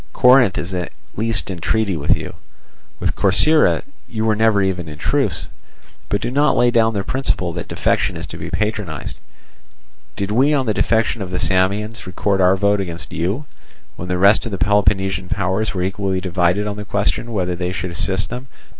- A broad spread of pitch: No, average, 3.3 semitones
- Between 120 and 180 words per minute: No, average, 190 wpm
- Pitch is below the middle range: Yes, low, 100 Hz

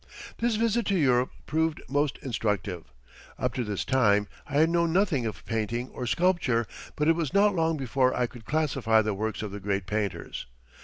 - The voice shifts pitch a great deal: Yes, wide, 7.0 semitones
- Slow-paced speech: No, average, 190 wpm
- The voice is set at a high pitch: No, low, 130 Hz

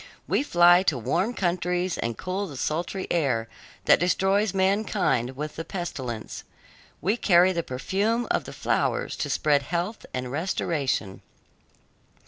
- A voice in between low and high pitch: Yes, medium, 175 Hz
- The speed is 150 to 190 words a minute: No, slow, 135 wpm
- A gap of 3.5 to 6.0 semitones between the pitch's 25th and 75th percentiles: Yes, wide, 5.4 semitones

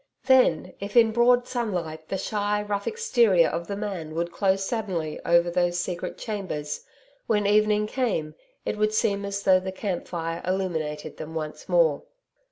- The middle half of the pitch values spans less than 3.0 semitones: No, average, 4.0 semitones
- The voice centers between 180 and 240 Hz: Yes, high, 190 Hz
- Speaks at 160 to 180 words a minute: Yes, average, 165 wpm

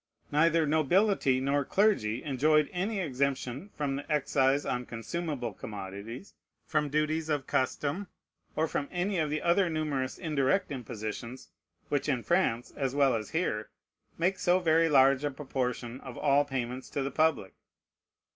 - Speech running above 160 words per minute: No, average, 145 wpm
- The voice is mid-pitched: Yes, medium, 145 Hz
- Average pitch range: Yes, average, 3.7 semitones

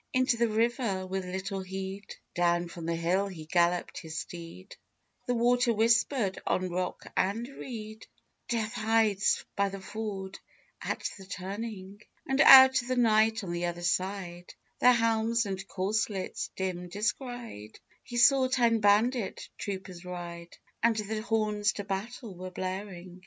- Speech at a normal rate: Yes, average, 145 wpm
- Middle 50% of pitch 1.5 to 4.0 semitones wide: Yes, average, 3.6 semitones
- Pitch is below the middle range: No, high, 200 Hz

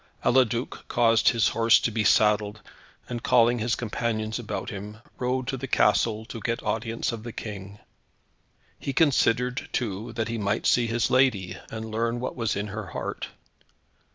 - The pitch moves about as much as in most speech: No, narrow, 2.1 semitones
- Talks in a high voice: No, low, 115 Hz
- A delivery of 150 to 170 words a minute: Yes, average, 165 wpm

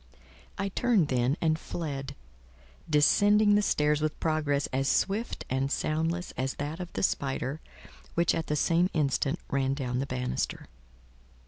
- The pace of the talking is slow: No, average, 145 wpm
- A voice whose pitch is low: No, medium, 150 Hz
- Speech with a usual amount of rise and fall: Yes, average, 3.9 semitones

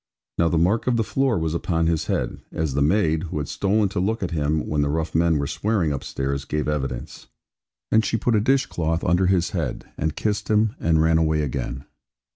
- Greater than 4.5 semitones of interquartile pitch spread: Yes, average, 5.0 semitones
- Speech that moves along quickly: Yes, fast, 220 wpm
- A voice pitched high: No, very low, 80 Hz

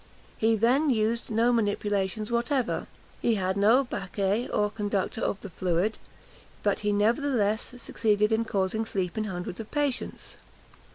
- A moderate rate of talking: No, slow, 130 wpm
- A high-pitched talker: Yes, high, 215 Hz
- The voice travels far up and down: No, average, 2.7 semitones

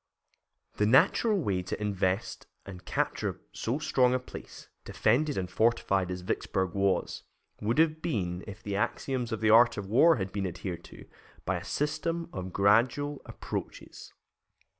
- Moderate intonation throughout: No, wide, 5.7 semitones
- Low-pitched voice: Yes, low, 105 Hz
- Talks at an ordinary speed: Yes, average, 155 wpm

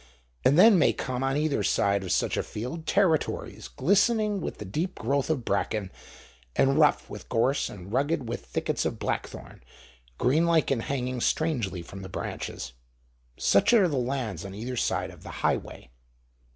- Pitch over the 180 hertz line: No, low, 130 Hz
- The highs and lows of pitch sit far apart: Yes, wide, 7.1 semitones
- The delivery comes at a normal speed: Yes, average, 165 wpm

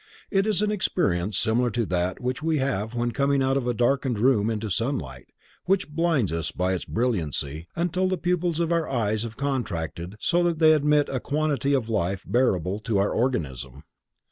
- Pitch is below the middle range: Yes, low, 125 Hz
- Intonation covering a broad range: Yes, wide, 7.7 semitones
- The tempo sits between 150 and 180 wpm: No, average, 190 wpm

